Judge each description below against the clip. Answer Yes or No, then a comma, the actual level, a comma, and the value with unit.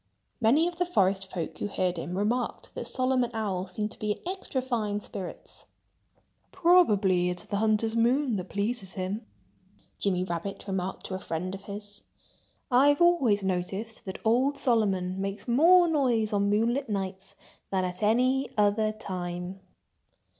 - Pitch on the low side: No, high, 210 Hz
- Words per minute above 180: No, average, 155 wpm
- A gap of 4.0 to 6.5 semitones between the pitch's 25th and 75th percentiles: Yes, average, 4.5 semitones